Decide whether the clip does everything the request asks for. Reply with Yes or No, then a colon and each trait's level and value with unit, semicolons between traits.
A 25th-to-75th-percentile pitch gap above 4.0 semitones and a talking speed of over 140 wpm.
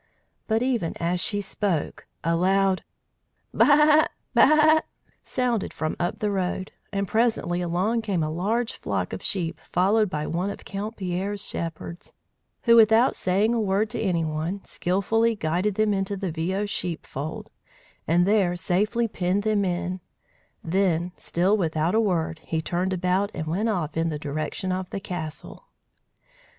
No: average, 3.6 semitones; average, 155 wpm